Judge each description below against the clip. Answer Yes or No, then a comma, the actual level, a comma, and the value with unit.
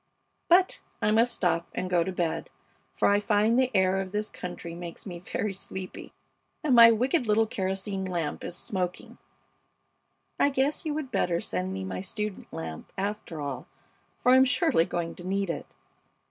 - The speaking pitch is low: No, high, 195 Hz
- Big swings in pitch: No, average, 4.7 semitones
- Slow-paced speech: No, average, 175 wpm